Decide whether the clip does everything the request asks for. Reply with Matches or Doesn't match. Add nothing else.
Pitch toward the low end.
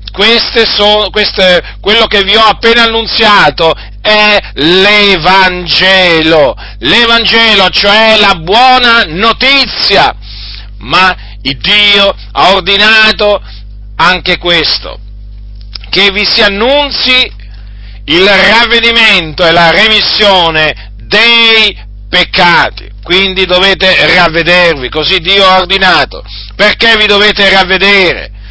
Doesn't match